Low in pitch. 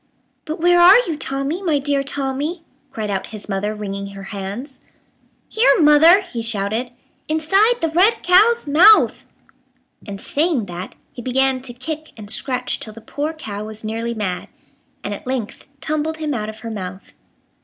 No: very high, 265 Hz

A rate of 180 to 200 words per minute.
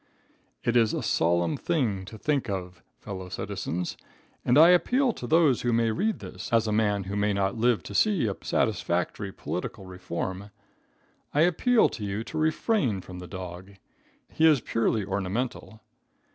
No: average, 165 wpm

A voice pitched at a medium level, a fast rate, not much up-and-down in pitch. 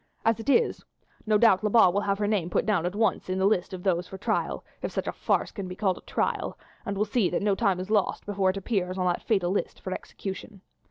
No: high, 195 Hz; fast, 260 wpm; narrow, 2.3 semitones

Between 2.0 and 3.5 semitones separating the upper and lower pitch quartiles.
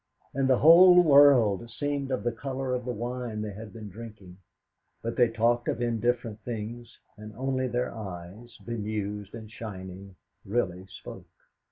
Yes: average, 3.0 semitones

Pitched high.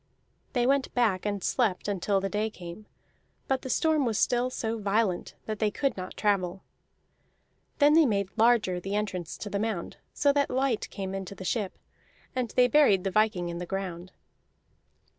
Yes: high, 210 Hz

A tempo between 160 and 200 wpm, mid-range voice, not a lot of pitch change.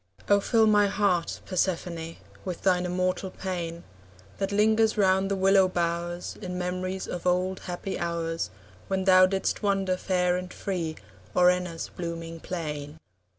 No: average, 145 wpm; medium, 180 Hz; narrow, 2.0 semitones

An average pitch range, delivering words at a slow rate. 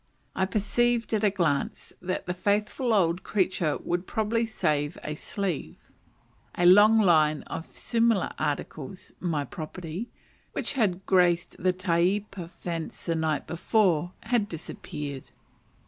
Yes: average, 4.1 semitones; slow, 130 wpm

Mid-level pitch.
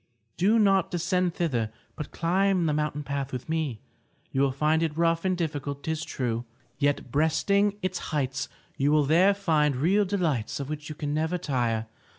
Yes: medium, 155 Hz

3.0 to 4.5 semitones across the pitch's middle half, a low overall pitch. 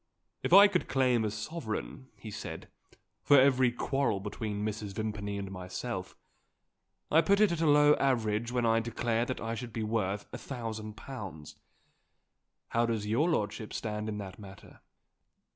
Yes: average, 3.9 semitones; low, 115 Hz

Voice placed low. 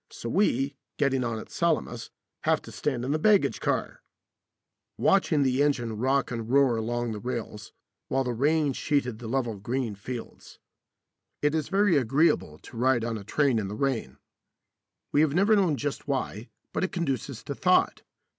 Yes: low, 130 Hz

